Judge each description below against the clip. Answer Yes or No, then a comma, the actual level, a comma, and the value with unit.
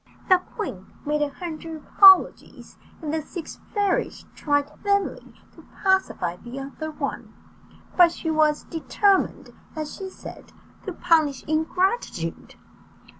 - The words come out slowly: Yes, slow, 125 wpm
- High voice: Yes, very high, 320 Hz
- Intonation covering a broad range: No, average, 4.2 semitones